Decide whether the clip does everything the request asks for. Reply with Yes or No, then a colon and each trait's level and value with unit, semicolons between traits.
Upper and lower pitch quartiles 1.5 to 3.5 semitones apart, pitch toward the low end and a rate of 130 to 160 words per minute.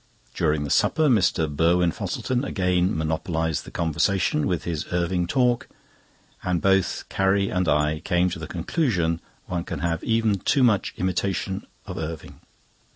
Yes: average, 3.2 semitones; very low, 90 Hz; average, 150 wpm